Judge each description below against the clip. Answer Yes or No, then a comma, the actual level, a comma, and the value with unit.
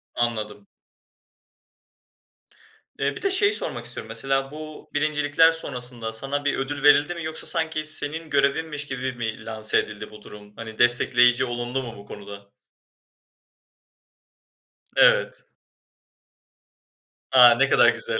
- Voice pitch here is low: Yes, low, 130 Hz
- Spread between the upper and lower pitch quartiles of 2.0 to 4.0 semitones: No, average, 4.7 semitones